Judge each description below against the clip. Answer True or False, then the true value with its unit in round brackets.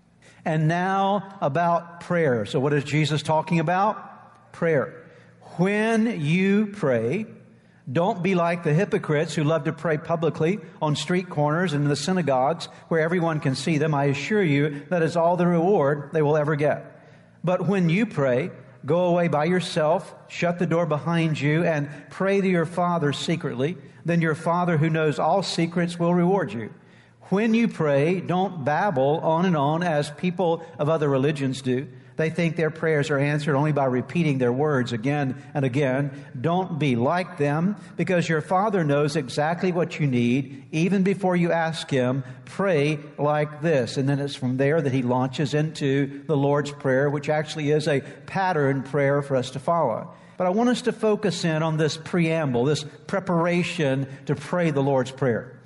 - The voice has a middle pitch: True (155 Hz)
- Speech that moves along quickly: False (175 wpm)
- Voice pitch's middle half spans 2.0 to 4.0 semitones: True (3.4 semitones)